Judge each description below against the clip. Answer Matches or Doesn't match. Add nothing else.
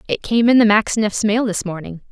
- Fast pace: Matches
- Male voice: Doesn't match